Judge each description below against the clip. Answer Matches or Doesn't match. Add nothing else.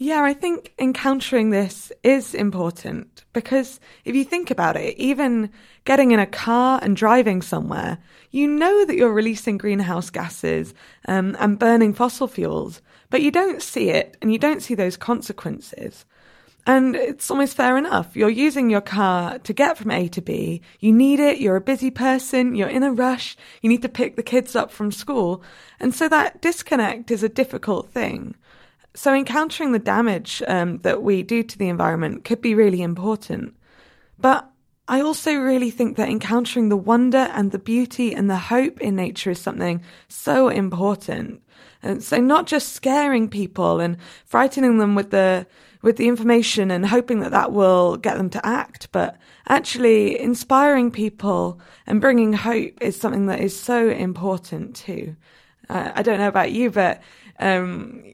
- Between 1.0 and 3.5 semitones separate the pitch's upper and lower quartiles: Doesn't match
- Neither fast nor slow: Matches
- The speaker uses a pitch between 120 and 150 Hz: Doesn't match